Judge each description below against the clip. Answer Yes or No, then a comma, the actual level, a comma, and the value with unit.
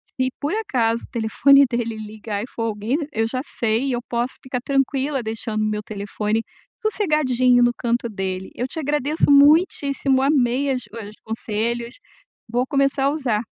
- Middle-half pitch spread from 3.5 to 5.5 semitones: Yes, average, 3.8 semitones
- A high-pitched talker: Yes, high, 245 Hz